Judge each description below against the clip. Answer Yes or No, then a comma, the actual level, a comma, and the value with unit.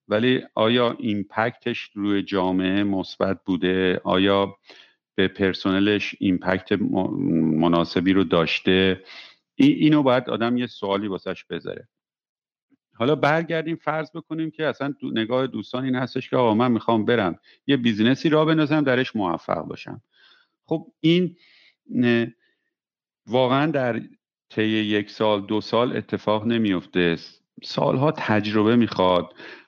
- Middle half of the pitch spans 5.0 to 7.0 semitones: Yes, wide, 5.4 semitones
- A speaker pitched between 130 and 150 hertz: No, low, 110 Hz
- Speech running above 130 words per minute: No, average, 120 wpm